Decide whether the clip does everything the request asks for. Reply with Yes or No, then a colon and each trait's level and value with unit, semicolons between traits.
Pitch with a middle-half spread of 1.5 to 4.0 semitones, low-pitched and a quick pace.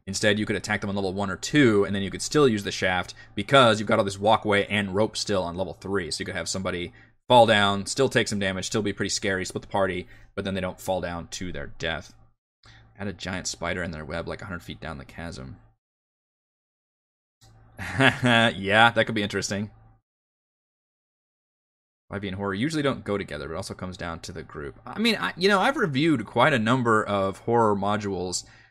Yes: average, 3.2 semitones; low, 100 Hz; fast, 215 wpm